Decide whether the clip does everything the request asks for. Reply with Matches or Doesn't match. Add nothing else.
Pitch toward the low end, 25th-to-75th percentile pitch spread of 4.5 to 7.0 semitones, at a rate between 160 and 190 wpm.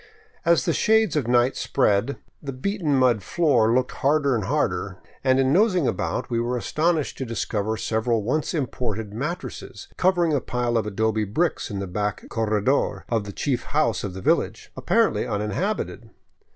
Matches